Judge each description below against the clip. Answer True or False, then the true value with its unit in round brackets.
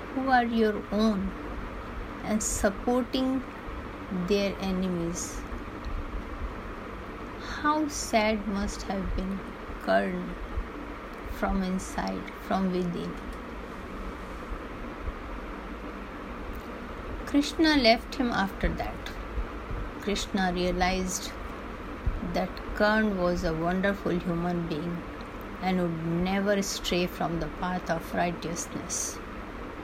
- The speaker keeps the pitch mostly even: False (3.8 semitones)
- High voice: True (195 Hz)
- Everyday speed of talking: False (80 wpm)